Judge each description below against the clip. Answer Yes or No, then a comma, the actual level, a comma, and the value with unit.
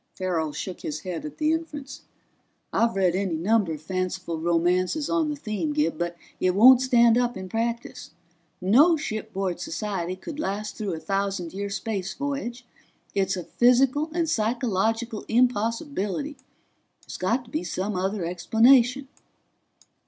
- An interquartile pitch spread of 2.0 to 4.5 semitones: No, wide, 5.4 semitones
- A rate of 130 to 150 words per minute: Yes, average, 145 wpm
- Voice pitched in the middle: No, high, 215 Hz